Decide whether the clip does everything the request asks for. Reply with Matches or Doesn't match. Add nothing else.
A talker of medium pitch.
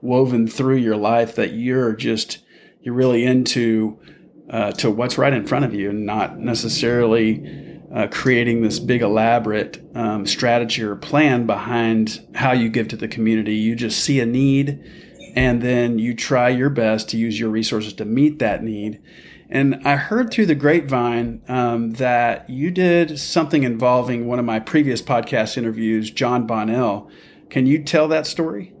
Doesn't match